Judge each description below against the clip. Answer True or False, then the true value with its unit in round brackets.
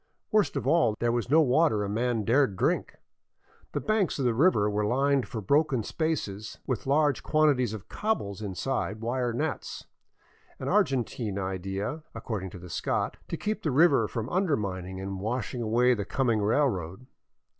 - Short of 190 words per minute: True (170 wpm)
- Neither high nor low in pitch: False (120 Hz)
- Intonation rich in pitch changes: True (5.7 semitones)